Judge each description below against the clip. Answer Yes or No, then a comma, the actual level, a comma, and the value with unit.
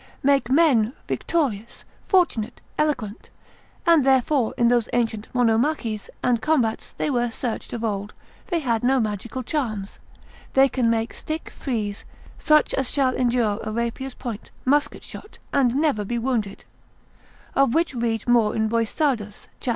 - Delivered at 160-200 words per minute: No, average, 145 wpm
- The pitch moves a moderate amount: Yes, average, 3.6 semitones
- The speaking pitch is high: Yes, high, 240 Hz